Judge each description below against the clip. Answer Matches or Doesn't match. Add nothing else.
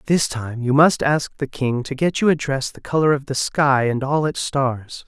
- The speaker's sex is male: Matches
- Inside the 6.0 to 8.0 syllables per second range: Doesn't match